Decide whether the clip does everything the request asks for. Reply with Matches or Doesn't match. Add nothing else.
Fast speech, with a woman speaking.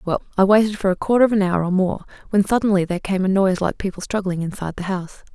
Matches